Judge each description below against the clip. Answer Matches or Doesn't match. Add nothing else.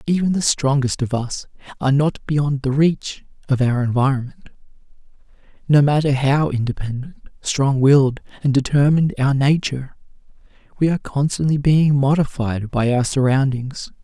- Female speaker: Doesn't match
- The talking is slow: Matches